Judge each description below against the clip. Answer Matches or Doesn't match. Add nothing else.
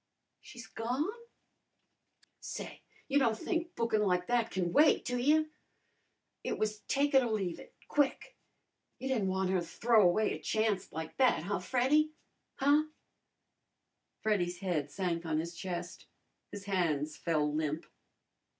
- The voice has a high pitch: Matches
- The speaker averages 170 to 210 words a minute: Doesn't match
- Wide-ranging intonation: Matches